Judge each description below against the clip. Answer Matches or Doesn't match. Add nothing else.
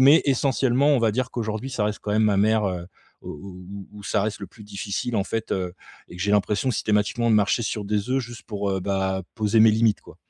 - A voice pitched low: Matches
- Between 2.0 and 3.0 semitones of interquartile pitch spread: Matches